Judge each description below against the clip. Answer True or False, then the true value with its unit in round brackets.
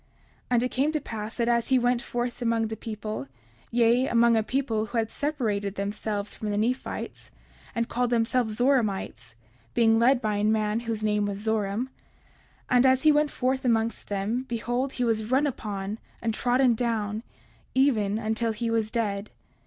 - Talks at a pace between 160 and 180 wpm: True (175 wpm)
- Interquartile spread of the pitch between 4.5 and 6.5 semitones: False (2.5 semitones)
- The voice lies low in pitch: False (230 Hz)